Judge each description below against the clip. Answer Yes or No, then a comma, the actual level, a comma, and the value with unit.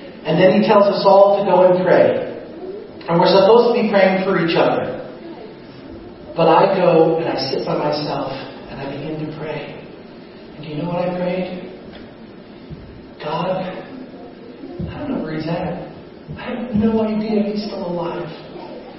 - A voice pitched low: No, medium, 185 Hz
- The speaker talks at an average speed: Yes, average, 165 wpm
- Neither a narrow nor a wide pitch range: Yes, average, 3.4 semitones